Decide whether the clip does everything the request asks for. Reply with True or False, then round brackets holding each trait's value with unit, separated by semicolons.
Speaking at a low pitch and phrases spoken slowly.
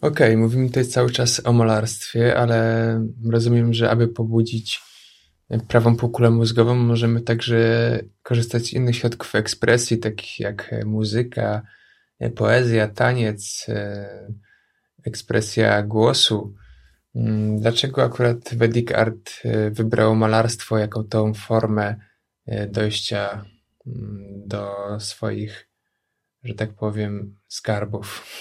True (115 Hz; 95 wpm)